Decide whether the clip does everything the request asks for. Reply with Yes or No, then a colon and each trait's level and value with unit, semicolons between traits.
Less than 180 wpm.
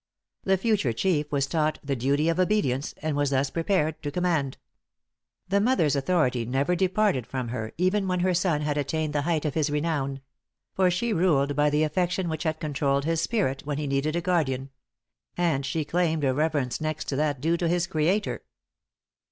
No: average, 190 wpm